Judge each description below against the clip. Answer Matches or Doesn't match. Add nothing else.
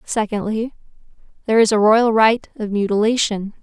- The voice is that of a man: Doesn't match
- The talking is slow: Matches